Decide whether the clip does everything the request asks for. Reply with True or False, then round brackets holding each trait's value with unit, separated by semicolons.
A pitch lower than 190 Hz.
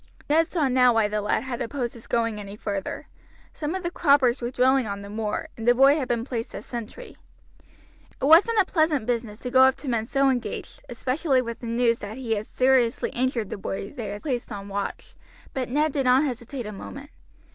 False (245 Hz)